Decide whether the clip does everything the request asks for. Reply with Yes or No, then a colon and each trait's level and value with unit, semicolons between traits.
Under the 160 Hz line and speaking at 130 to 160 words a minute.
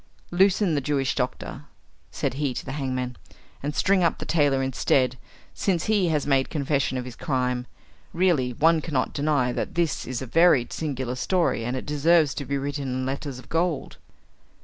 No: medium, 140 Hz; average, 180 wpm